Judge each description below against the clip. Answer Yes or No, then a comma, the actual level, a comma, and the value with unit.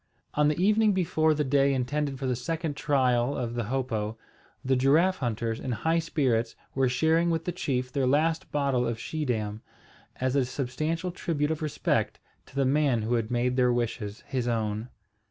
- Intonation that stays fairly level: No, average, 4.1 semitones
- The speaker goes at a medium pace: Yes, average, 180 wpm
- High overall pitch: No, low, 135 Hz